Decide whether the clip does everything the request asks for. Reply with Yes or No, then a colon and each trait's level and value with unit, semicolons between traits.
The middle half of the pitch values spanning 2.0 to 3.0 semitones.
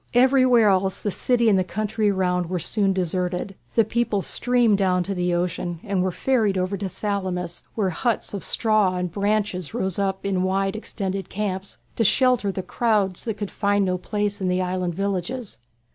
Yes: narrow, 2.6 semitones